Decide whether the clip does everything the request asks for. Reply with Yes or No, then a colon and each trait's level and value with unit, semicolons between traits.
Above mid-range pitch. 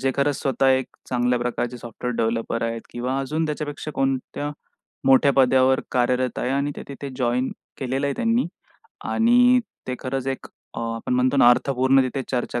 No: low, 130 Hz